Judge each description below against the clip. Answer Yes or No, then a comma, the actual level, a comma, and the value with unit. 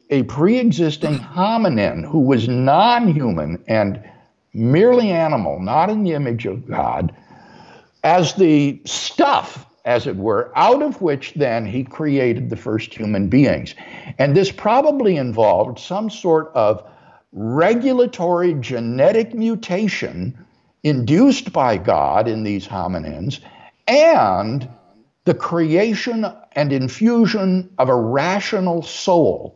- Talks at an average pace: No, slow, 120 wpm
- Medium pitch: Yes, medium, 155 Hz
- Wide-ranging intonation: Yes, wide, 8.4 semitones